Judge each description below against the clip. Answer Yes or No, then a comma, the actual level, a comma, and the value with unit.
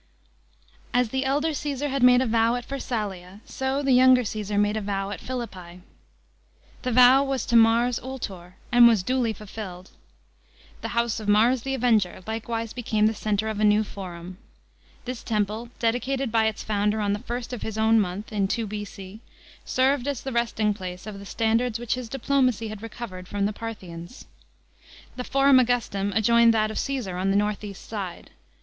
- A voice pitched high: Yes, high, 225 Hz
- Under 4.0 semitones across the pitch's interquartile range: Yes, average, 3.4 semitones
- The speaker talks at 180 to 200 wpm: Yes, average, 185 wpm